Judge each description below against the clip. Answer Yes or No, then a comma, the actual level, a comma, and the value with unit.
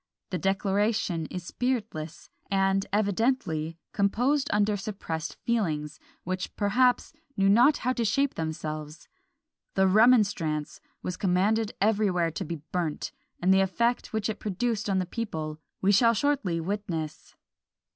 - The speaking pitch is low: No, high, 195 Hz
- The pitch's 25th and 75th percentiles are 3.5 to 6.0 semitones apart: Yes, average, 4.6 semitones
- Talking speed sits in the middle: No, slow, 130 wpm